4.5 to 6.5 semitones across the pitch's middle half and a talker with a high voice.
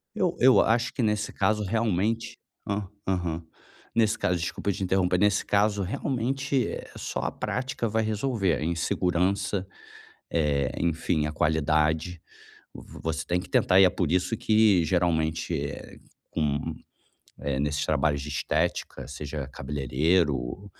No: average, 5.2 semitones; very low, 90 Hz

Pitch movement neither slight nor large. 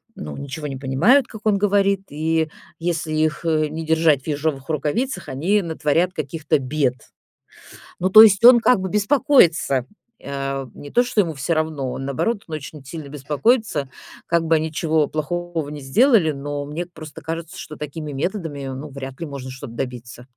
Yes: average, 3.9 semitones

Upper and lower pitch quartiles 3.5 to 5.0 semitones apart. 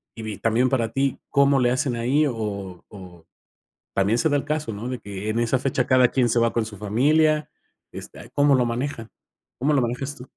Yes: average, 3.9 semitones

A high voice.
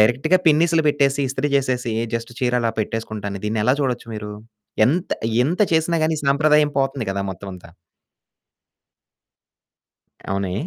No: low, 130 Hz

